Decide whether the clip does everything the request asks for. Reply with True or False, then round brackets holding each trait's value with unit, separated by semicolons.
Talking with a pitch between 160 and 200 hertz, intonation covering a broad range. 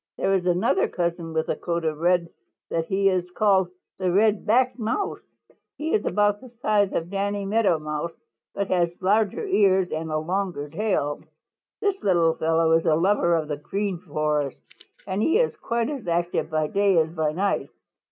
False (185 Hz; 4.0 semitones)